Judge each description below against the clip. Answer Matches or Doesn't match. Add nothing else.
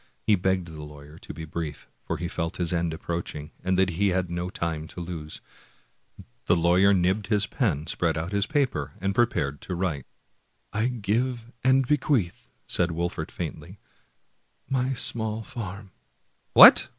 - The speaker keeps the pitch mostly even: Doesn't match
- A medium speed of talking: Matches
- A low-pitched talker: Matches